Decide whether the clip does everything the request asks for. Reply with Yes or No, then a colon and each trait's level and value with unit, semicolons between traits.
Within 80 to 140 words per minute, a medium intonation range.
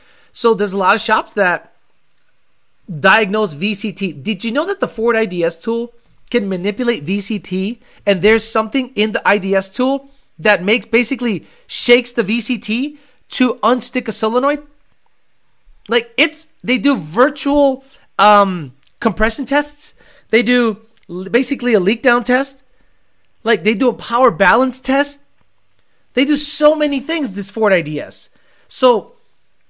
Yes: slow, 135 wpm; average, 3.9 semitones